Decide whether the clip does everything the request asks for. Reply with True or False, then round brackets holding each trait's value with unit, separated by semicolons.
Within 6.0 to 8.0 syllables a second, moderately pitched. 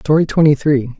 False (5.7 syllables/s; 145 Hz)